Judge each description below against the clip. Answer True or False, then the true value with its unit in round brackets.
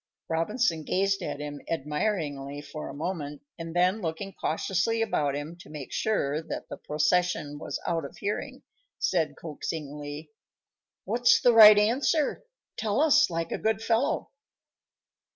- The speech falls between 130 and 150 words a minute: True (140 wpm)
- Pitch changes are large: True (6.0 semitones)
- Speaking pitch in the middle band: True (165 Hz)